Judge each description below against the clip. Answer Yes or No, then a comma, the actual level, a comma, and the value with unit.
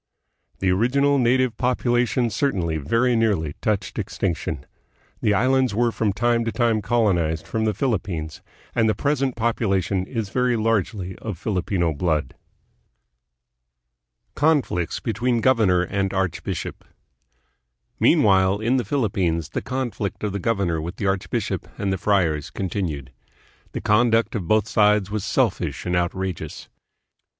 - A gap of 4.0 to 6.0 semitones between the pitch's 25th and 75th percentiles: Yes, average, 4.4 semitones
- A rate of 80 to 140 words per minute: Yes, slow, 135 wpm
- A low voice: Yes, low, 105 Hz